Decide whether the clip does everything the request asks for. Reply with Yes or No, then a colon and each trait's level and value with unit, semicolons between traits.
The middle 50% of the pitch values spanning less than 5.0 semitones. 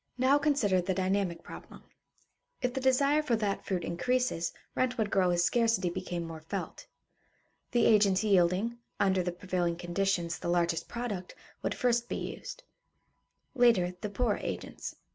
No: average, 5.3 semitones